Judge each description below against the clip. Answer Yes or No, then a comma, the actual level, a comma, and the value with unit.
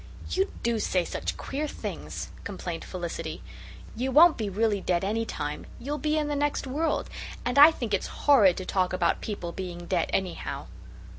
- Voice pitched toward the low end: No, high, 215 Hz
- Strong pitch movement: Yes, wide, 7.7 semitones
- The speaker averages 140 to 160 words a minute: No, average, 175 wpm